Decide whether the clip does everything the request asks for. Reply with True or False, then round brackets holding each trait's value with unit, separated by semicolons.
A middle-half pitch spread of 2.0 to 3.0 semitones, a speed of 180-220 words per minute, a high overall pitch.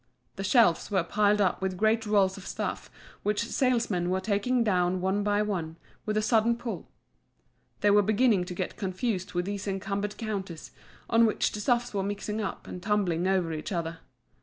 True (2.6 semitones; 185 wpm; 200 Hz)